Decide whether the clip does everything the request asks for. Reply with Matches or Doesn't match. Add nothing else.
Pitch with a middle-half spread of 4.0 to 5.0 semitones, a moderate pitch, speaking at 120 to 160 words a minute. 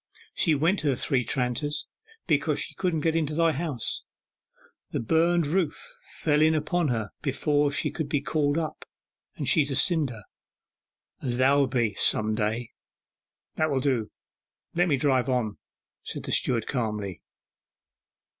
Matches